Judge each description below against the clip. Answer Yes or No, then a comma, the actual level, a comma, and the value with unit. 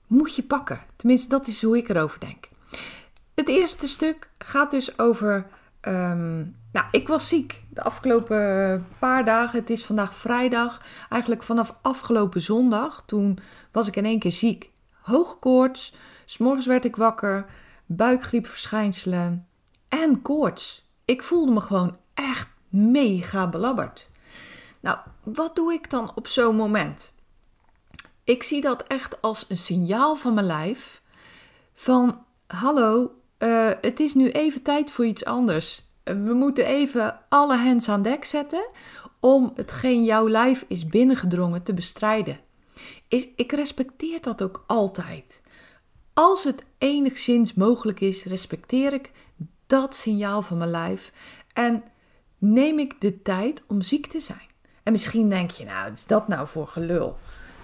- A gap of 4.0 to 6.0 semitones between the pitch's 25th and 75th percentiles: Yes, average, 4.9 semitones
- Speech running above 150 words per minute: No, average, 145 wpm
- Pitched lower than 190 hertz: No, high, 230 Hz